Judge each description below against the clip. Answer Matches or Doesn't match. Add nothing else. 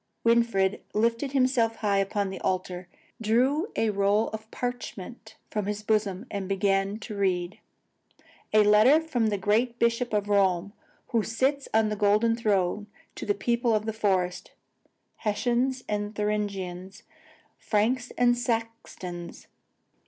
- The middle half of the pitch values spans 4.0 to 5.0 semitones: Doesn't match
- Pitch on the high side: Matches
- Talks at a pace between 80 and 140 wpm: Matches